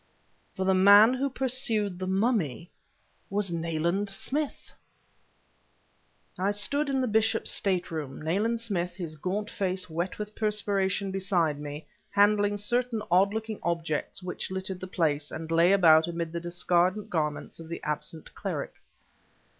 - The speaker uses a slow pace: No, average, 145 wpm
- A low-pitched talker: No, high, 190 Hz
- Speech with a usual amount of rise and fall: Yes, average, 3.9 semitones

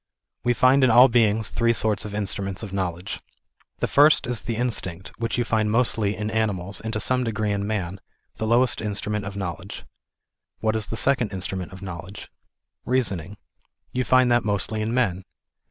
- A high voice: No, low, 110 Hz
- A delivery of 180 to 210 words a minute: Yes, average, 185 wpm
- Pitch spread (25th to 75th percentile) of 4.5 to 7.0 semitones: No, average, 3.3 semitones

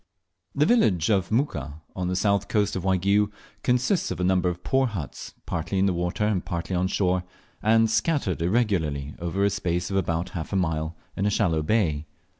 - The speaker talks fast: No, average, 195 wpm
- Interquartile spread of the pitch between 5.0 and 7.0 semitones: No, average, 3.6 semitones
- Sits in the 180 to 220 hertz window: No, very low, 95 Hz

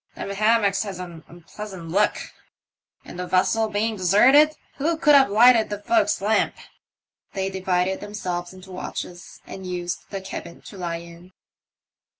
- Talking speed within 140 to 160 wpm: Yes, average, 155 wpm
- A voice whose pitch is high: Yes, high, 195 Hz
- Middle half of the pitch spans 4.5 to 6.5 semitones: No, average, 3.3 semitones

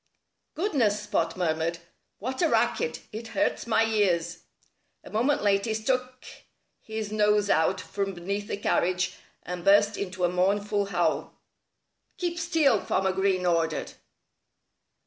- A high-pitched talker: Yes, high, 205 Hz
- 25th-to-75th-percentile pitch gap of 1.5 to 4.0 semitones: Yes, average, 3.6 semitones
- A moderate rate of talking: No, slow, 130 wpm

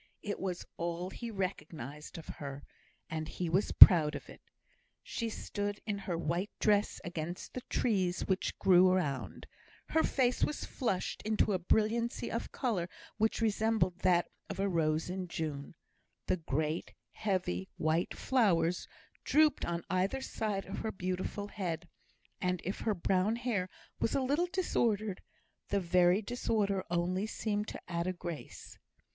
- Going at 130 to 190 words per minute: Yes, average, 150 wpm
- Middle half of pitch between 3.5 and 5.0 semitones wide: Yes, average, 3.9 semitones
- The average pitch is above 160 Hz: Yes, medium, 185 Hz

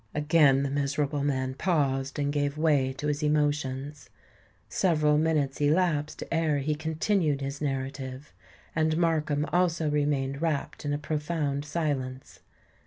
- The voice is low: No, medium, 145 Hz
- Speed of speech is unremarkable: No, slow, 130 wpm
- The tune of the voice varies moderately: No, narrow, 2.0 semitones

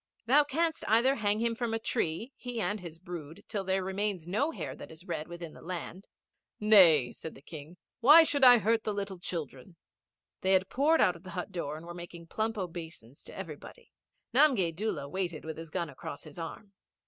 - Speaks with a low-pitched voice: No, medium, 185 Hz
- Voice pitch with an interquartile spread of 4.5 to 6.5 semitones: Yes, average, 5.2 semitones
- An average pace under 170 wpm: No, fast, 205 wpm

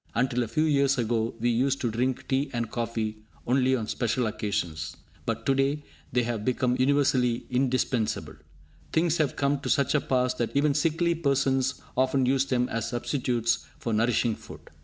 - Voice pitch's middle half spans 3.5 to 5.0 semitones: No, average, 2.7 semitones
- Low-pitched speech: Yes, low, 125 Hz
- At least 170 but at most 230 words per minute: Yes, average, 175 wpm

